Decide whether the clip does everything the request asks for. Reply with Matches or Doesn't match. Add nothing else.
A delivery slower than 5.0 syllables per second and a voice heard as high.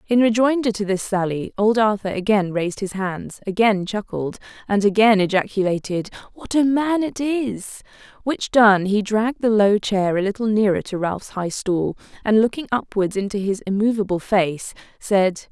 Matches